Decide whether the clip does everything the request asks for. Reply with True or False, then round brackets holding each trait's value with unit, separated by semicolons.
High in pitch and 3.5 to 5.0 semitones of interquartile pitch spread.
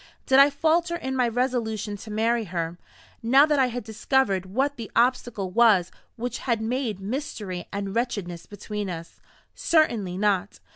True (225 Hz; 4.5 semitones)